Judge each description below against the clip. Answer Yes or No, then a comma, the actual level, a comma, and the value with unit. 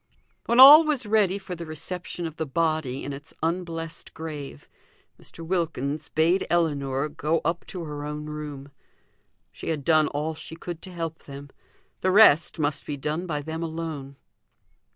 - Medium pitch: Yes, medium, 160 Hz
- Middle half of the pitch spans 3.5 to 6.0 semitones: No, average, 2.7 semitones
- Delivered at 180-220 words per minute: No, average, 165 wpm